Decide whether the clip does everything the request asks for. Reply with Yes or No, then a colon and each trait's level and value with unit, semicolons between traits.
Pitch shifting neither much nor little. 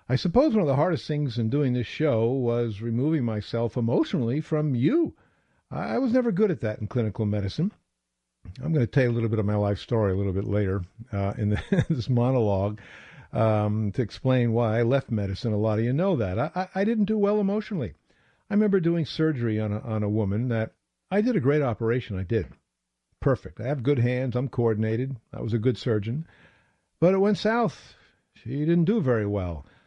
No: wide, 6.2 semitones